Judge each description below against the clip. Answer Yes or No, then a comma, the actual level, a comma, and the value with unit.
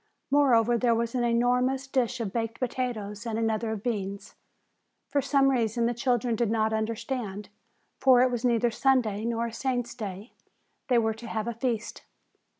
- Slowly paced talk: No, average, 170 wpm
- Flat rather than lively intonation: Yes, narrow, 2.2 semitones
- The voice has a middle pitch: No, high, 235 Hz